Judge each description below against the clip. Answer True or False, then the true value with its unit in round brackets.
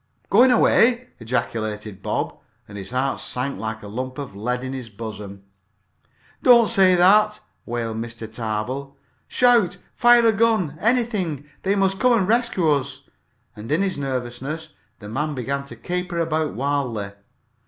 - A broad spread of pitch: True (8.8 semitones)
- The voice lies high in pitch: False (140 Hz)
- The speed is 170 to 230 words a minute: False (150 wpm)